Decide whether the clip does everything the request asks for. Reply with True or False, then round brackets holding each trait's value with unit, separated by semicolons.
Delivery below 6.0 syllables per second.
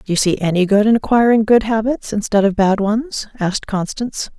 True (5.5 syllables/s)